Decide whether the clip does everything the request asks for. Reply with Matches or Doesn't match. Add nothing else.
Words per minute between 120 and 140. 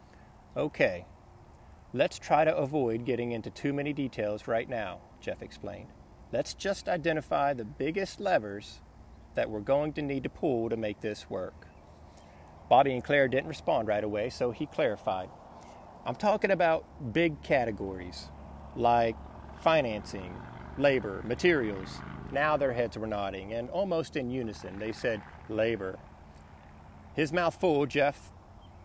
Matches